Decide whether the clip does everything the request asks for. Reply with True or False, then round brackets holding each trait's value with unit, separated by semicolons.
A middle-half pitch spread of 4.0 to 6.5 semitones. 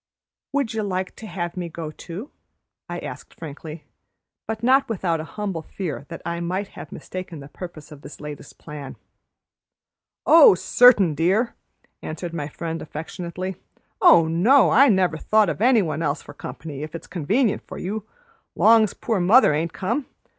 True (5.3 semitones)